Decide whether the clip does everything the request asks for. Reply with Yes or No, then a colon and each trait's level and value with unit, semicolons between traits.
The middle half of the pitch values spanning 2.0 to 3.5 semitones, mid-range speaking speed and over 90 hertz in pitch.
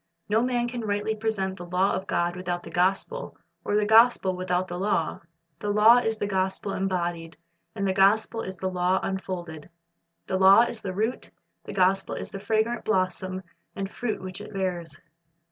Yes: average, 2.8 semitones; average, 180 wpm; high, 190 Hz